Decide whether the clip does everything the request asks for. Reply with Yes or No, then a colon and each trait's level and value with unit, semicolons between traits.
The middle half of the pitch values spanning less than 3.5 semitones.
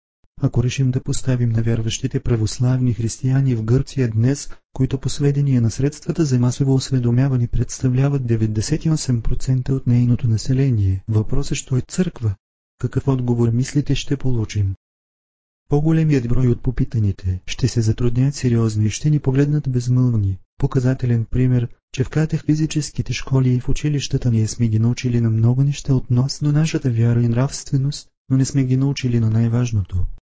Yes: average, 2.9 semitones